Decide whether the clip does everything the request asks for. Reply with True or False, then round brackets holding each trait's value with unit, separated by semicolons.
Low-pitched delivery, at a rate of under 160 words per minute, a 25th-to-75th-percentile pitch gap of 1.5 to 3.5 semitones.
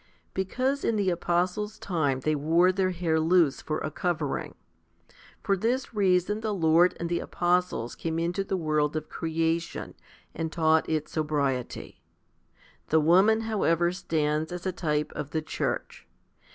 False (170 Hz; 150 wpm; 3.1 semitones)